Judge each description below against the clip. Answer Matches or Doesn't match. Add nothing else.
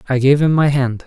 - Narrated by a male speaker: Matches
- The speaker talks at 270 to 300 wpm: Matches